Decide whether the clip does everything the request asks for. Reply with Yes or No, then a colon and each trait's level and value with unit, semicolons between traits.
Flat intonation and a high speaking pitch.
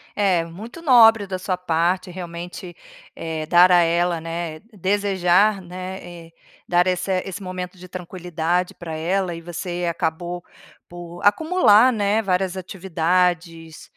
No: narrow, 1.9 semitones; medium, 180 Hz